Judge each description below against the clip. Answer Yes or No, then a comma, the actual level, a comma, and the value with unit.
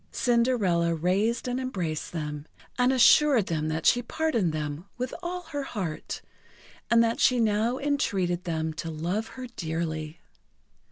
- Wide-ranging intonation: Yes, wide, 7.4 semitones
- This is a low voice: No, high, 195 Hz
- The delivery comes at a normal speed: Yes, average, 145 wpm